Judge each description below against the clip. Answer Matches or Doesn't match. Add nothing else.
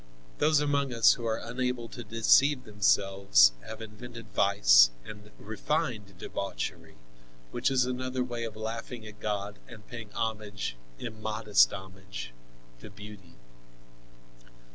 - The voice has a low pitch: Matches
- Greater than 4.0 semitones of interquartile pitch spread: Doesn't match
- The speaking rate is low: Matches